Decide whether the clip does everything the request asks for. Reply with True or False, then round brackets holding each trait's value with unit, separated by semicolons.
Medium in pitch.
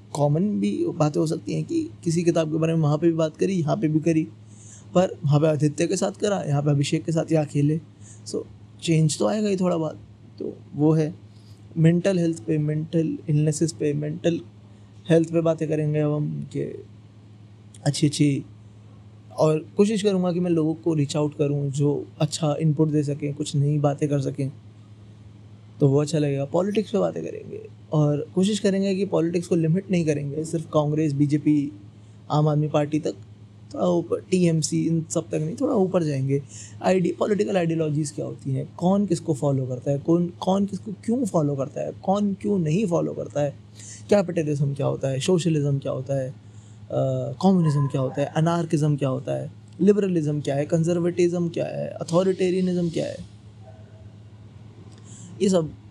True (150 Hz)